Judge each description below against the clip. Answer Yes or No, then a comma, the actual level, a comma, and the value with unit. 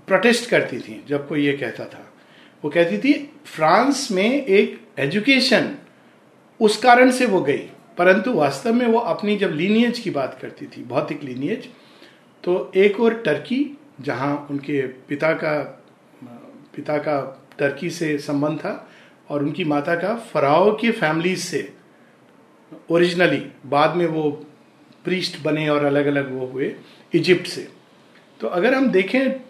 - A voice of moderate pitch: Yes, medium, 175 Hz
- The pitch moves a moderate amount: No, wide, 7.7 semitones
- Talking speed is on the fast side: No, average, 145 wpm